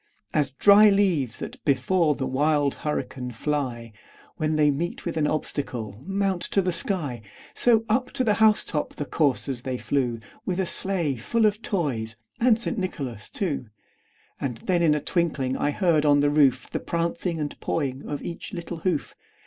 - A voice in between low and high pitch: Yes, medium, 150 Hz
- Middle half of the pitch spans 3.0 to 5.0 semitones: No, wide, 5.6 semitones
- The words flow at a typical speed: Yes, average, 175 wpm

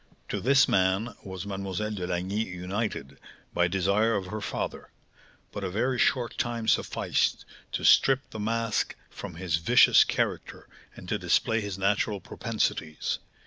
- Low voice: Yes, low, 100 Hz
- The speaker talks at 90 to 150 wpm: Yes, average, 145 wpm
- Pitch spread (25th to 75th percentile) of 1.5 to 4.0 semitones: Yes, average, 3.4 semitones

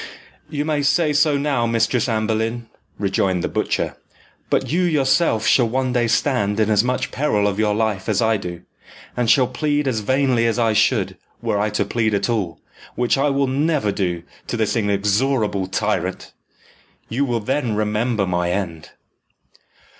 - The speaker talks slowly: No, average, 170 wpm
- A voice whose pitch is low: Yes, low, 115 Hz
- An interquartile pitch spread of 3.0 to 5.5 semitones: Yes, average, 4.5 semitones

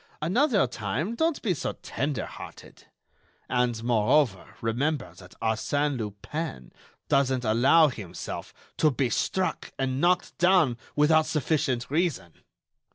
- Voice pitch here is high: No, low, 135 Hz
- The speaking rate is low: Yes, slow, 115 wpm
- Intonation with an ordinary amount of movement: No, wide, 5.7 semitones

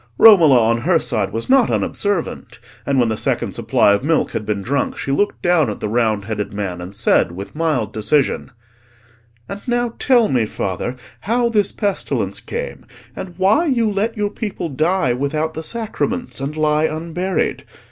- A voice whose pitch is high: No, medium, 155 Hz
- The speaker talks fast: No, average, 175 wpm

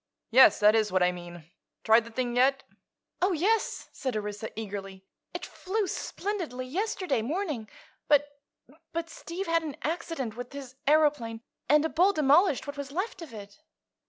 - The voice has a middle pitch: No, very high, 275 Hz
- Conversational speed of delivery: Yes, average, 160 wpm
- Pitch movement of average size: No, wide, 6.9 semitones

